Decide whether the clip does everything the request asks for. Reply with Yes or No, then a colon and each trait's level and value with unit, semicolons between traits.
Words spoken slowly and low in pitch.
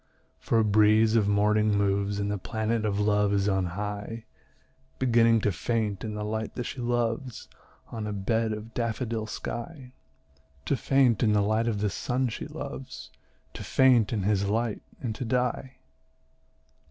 No: average, 165 wpm; low, 110 Hz